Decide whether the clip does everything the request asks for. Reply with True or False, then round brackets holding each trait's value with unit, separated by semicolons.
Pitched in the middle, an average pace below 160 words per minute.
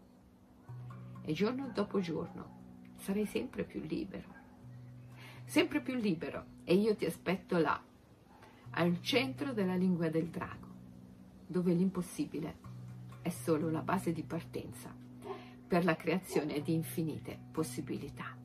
True (150 Hz; 115 wpm)